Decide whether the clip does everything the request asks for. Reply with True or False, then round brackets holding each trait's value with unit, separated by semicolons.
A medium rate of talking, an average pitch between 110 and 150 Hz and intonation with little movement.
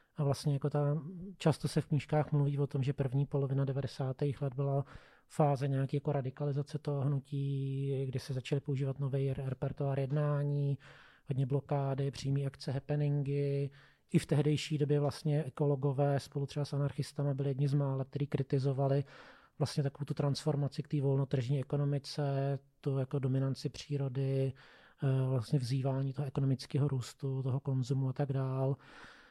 True (150 wpm; 140 Hz; 1.1 semitones)